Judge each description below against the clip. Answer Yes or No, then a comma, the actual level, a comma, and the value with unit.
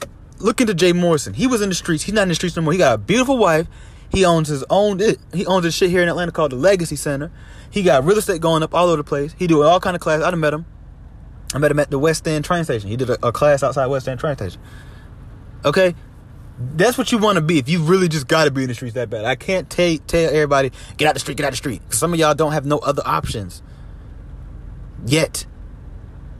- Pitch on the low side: No, medium, 155 Hz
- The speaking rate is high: Yes, fast, 265 wpm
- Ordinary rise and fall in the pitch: Yes, average, 4.8 semitones